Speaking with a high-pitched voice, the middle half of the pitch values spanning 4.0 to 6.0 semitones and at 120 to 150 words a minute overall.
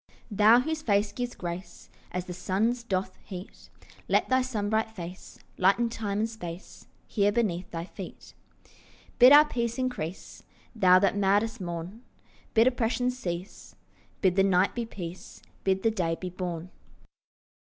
Yes: high, 205 Hz; average, 4.3 semitones; average, 145 wpm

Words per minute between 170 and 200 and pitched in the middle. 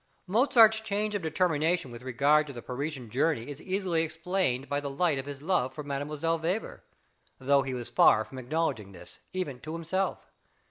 Yes: average, 180 wpm; medium, 150 Hz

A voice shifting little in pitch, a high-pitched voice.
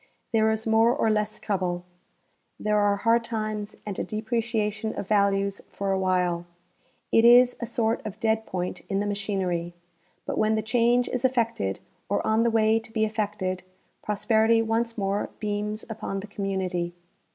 Yes: narrow, 2.2 semitones; high, 215 Hz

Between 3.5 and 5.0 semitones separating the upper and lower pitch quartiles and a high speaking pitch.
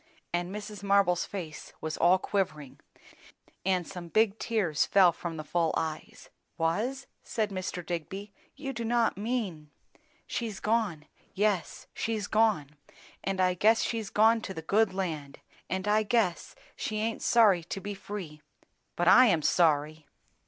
Yes: average, 4.2 semitones; high, 195 Hz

